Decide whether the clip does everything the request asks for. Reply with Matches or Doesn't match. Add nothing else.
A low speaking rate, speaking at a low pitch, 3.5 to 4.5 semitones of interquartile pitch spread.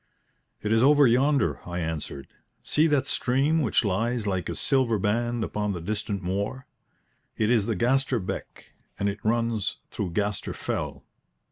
Doesn't match